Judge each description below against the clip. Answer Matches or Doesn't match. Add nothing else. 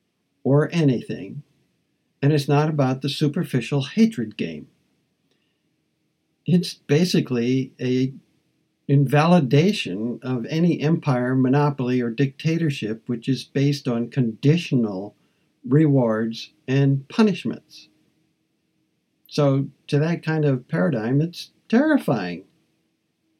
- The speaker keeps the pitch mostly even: Doesn't match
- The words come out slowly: Matches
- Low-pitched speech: Doesn't match